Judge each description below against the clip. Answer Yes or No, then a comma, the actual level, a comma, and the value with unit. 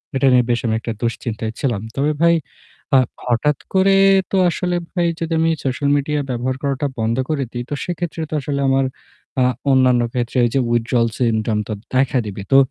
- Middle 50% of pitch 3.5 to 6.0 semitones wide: Yes, average, 4.0 semitones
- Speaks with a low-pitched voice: Yes, low, 130 Hz